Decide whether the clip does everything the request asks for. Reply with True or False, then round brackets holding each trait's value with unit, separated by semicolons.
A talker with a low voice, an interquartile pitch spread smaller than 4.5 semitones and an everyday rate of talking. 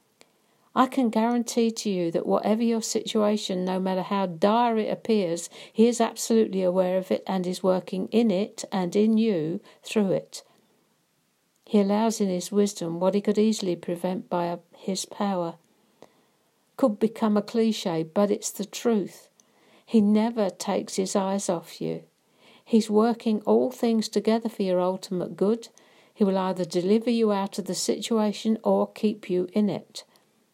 False (205 Hz; 3.1 semitones; 165 wpm)